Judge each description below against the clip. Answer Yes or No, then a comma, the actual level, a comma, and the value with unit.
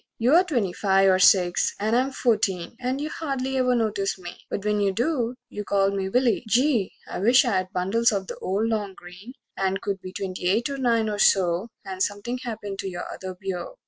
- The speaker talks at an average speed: No, fast, 210 wpm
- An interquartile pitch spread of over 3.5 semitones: Yes, average, 4.2 semitones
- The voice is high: Yes, high, 205 Hz